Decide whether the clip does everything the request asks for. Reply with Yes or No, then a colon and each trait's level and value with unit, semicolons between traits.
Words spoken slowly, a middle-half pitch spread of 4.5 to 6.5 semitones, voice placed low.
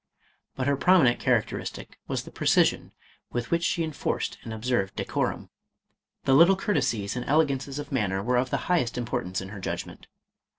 No: average, 175 wpm; average, 4.8 semitones; low, 125 Hz